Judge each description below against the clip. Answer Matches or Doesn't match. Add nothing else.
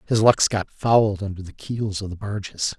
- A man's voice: Matches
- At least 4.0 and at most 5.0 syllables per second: Matches